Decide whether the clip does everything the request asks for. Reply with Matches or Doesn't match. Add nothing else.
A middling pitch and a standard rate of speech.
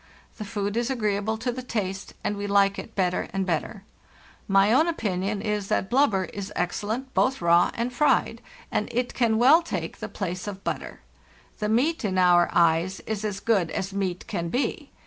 Doesn't match